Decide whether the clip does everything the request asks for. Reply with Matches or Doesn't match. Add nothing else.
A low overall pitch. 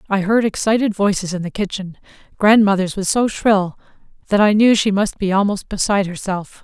Doesn't match